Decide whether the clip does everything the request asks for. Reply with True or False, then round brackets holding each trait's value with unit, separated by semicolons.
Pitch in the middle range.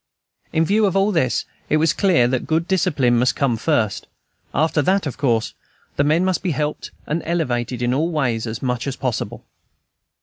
True (150 Hz)